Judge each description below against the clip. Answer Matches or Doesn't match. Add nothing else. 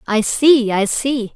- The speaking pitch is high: Matches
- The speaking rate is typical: Matches